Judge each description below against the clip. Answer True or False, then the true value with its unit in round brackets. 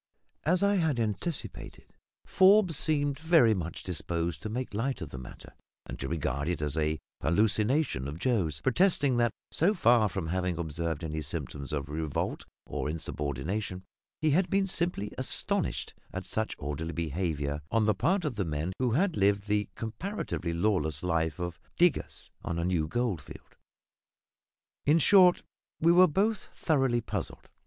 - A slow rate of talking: False (155 wpm)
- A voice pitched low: True (100 Hz)